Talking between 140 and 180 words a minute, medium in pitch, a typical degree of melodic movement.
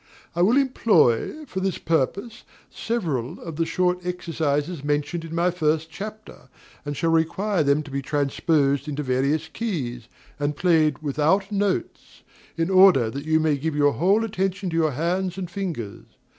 Yes: average, 160 wpm; medium, 165 Hz; average, 4.5 semitones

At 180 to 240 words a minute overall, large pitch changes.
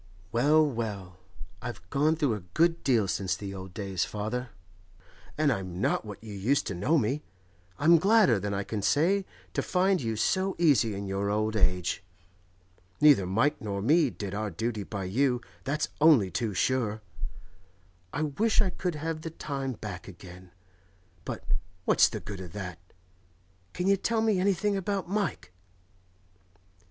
No: average, 160 wpm; wide, 7.9 semitones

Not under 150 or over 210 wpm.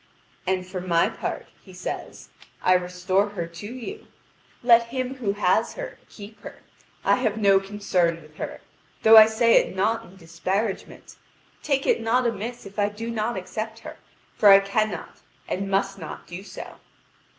Yes: average, 170 wpm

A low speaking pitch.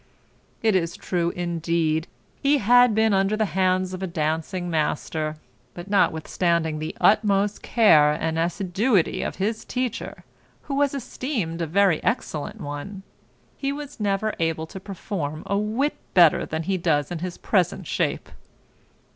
No: medium, 185 Hz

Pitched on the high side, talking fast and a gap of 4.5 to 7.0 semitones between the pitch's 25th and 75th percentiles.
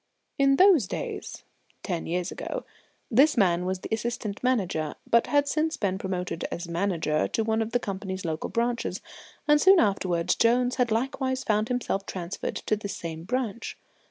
No: high, 215 Hz; average, 165 wpm; wide, 5.4 semitones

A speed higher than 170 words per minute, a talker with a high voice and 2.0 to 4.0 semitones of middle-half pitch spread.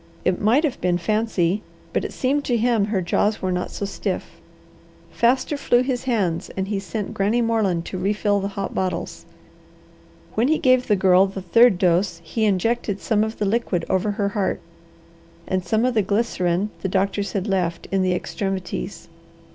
Yes: average, 180 wpm; high, 200 Hz; average, 3.5 semitones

